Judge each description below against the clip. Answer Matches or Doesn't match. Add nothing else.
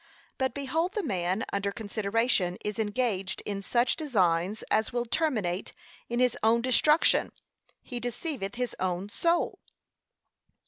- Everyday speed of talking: Doesn't match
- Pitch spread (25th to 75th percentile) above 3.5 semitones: Matches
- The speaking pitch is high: Matches